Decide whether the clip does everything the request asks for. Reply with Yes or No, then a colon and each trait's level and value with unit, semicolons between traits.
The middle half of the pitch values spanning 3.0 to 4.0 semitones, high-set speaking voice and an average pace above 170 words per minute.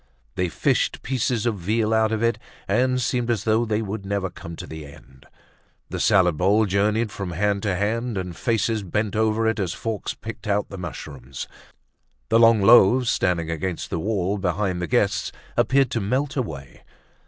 No: average, 3.7 semitones; low, 105 Hz; average, 180 wpm